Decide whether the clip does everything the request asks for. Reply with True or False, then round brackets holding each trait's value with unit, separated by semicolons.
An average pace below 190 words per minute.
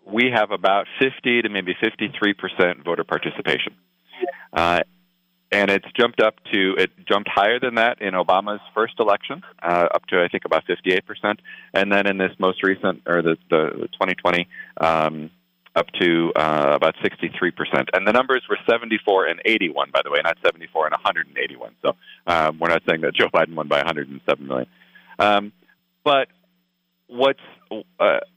True (165 wpm)